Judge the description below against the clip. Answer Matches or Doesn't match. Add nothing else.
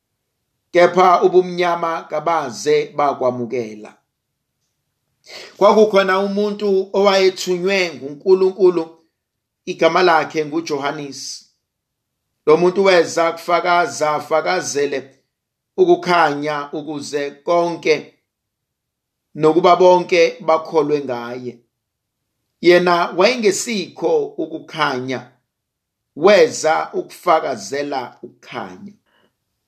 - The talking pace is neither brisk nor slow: Doesn't match